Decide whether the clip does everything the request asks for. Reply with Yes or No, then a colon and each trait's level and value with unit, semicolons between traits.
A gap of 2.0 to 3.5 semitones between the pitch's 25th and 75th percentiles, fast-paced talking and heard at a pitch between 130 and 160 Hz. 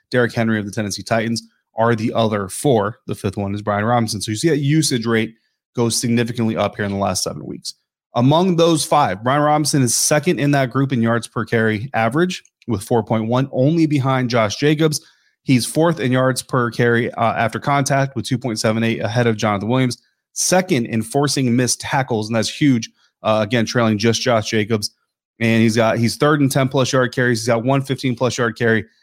No: average, 3.1 semitones; fast, 215 wpm; low, 120 Hz